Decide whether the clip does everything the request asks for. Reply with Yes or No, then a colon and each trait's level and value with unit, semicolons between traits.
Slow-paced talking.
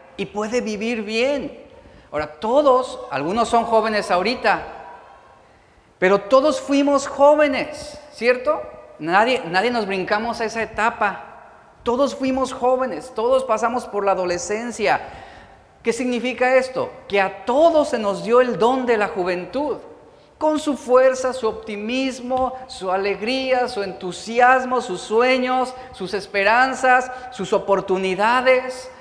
Yes: slow, 120 wpm